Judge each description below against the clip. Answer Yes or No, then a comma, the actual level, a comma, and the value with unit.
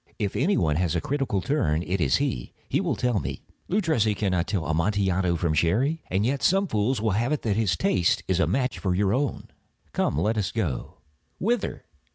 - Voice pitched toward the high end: No, low, 100 Hz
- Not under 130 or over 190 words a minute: No, average, 200 wpm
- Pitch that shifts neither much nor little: No, wide, 6.5 semitones